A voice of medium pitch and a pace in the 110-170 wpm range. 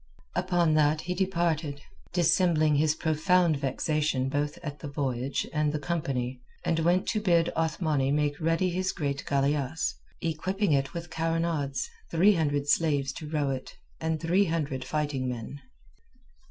Yes: medium, 155 Hz; average, 145 wpm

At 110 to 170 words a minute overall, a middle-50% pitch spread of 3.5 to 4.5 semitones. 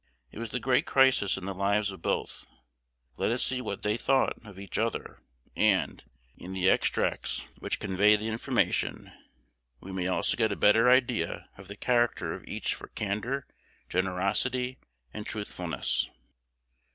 Yes: average, 155 wpm; average, 4.0 semitones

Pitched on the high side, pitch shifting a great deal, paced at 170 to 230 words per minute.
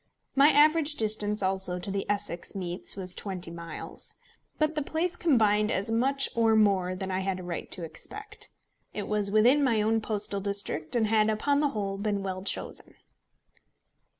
No: high, 210 Hz; average, 3.9 semitones; average, 175 wpm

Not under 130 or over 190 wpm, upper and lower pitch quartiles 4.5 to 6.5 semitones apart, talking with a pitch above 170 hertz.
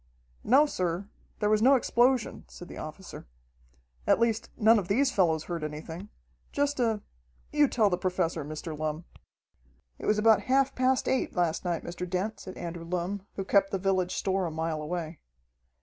Yes: average, 175 wpm; average, 4.8 semitones; high, 190 Hz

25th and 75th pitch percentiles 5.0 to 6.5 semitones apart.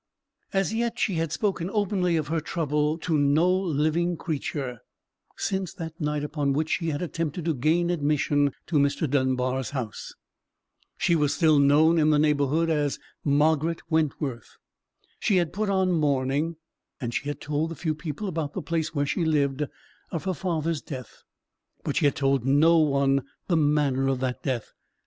No: average, 2.8 semitones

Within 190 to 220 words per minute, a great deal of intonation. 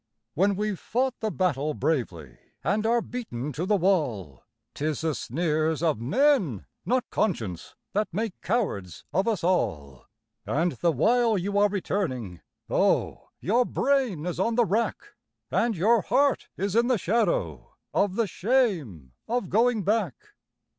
No: average, 145 wpm; wide, 7.3 semitones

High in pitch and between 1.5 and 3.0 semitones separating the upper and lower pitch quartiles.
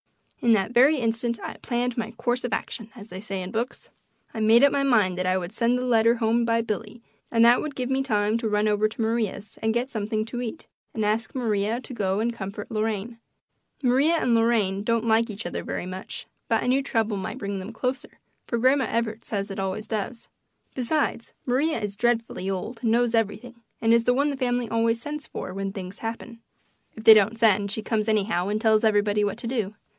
Yes: high, 225 Hz; narrow, 2.5 semitones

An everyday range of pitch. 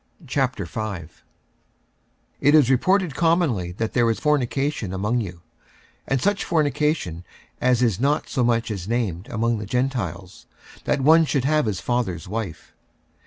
No: wide, 5.9 semitones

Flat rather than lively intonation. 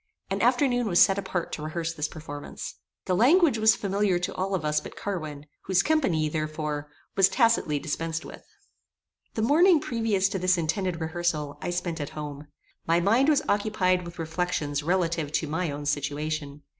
No: average, 4.6 semitones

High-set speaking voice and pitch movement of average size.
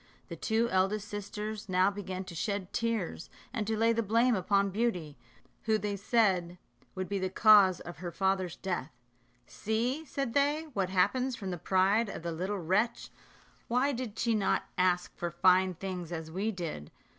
Yes: high, 195 Hz; average, 3.3 semitones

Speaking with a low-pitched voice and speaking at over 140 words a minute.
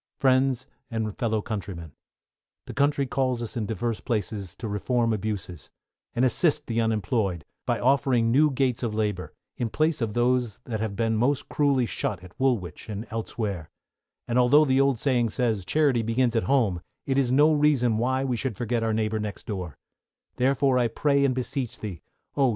Yes: low, 120 Hz; average, 180 wpm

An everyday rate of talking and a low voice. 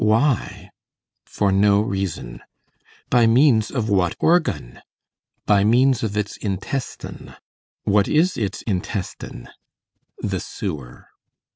No: slow, 105 wpm; low, 105 Hz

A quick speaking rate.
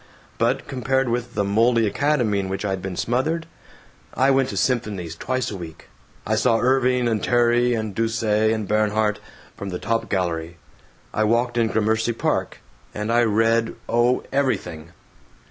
No: average, 165 wpm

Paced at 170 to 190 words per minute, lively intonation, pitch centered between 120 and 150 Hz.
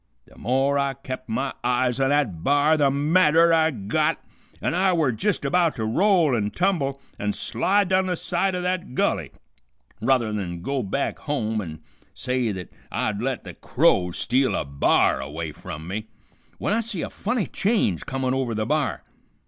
Yes: average, 180 wpm; wide, 7.2 semitones; low, 135 Hz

